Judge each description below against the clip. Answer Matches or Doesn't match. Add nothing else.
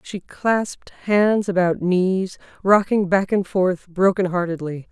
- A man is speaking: Doesn't match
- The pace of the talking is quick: Doesn't match